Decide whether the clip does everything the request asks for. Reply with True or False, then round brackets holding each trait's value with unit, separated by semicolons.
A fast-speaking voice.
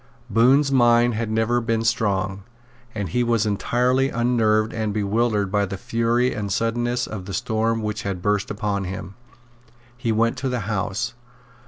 False (160 wpm)